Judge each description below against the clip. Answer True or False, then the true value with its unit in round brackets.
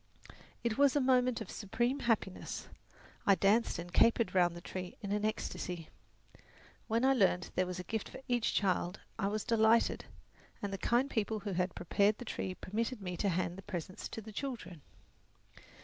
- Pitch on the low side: False (205 Hz)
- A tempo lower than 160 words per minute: False (185 wpm)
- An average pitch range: True (4.0 semitones)